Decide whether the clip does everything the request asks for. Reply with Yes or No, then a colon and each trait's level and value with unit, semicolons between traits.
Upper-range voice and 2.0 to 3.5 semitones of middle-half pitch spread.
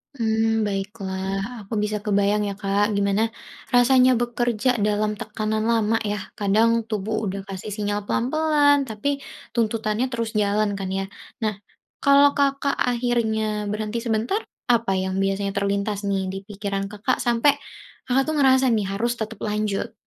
Yes: high, 215 Hz; average, 2.8 semitones